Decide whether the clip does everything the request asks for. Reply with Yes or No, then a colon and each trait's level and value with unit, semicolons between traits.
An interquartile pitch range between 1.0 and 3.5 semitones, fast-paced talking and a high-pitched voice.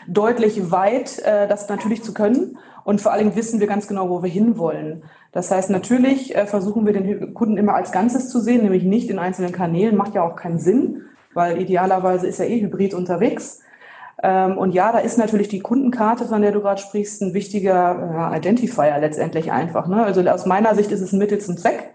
Yes: average, 3.2 semitones; fast, 195 wpm; high, 200 Hz